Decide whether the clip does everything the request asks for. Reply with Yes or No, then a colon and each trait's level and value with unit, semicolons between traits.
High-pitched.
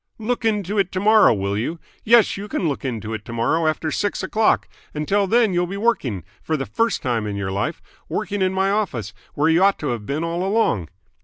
No: medium, 170 Hz